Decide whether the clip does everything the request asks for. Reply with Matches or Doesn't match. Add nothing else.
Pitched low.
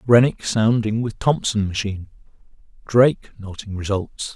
Matches